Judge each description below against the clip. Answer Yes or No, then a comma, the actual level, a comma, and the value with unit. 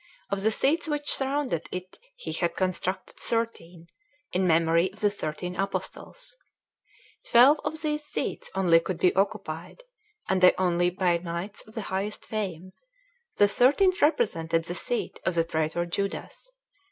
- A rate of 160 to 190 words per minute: No, average, 150 wpm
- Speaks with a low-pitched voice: No, high, 190 Hz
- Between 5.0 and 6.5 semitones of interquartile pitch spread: Yes, wide, 5.4 semitones